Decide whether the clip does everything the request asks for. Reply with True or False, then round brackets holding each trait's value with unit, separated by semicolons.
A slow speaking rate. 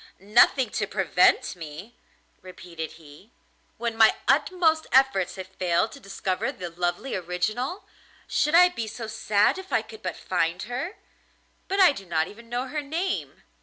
False (160 wpm)